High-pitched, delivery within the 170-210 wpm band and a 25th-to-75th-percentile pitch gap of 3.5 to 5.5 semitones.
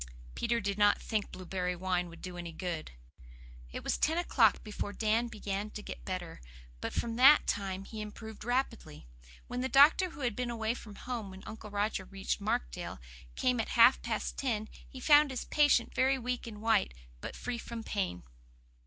Yes: high, 220 Hz; average, 185 wpm; average, 4.1 semitones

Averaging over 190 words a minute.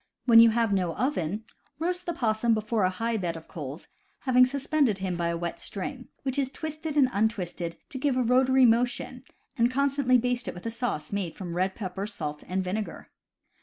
Yes: fast, 205 wpm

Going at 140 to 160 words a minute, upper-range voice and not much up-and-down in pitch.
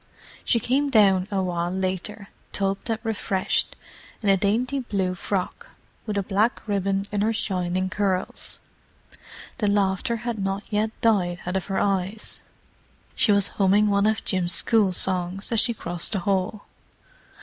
Yes: average, 155 wpm; high, 200 Hz; narrow, 2.3 semitones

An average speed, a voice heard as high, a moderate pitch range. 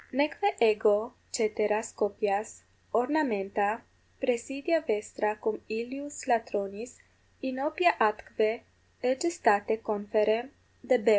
No: slow, 80 wpm; high, 225 Hz; average, 3.9 semitones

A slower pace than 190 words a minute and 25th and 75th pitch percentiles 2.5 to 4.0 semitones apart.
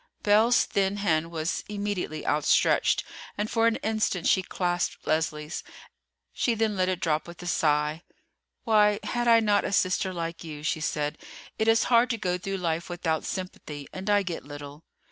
No: average, 170 wpm; average, 4.6 semitones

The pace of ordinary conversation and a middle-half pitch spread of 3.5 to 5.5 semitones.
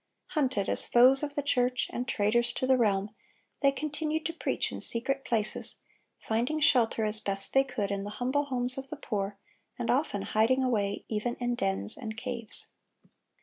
Yes: average, 180 wpm; average, 4.1 semitones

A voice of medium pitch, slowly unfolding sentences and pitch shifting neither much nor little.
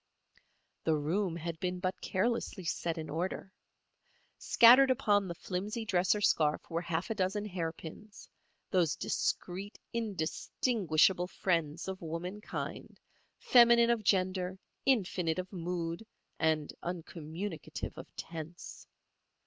Yes: medium, 180 Hz; slow, 110 wpm; average, 3.7 semitones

